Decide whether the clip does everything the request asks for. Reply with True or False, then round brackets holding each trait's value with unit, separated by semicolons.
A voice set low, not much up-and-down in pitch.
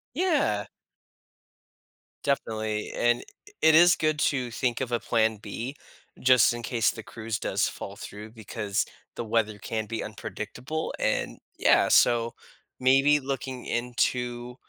False (120 Hz; 3.0 semitones)